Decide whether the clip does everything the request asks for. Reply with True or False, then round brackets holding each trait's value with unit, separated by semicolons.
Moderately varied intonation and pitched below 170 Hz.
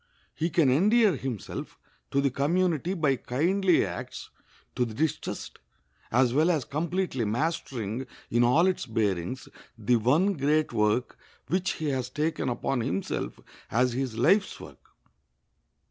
False (5.7 semitones; 135 Hz)